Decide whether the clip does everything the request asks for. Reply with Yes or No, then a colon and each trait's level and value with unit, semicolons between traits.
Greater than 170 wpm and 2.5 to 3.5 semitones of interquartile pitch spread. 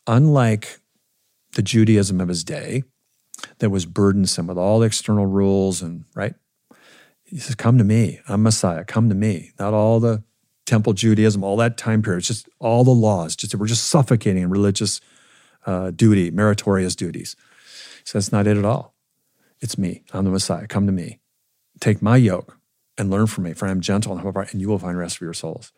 Yes: average, 200 wpm; average, 2.8 semitones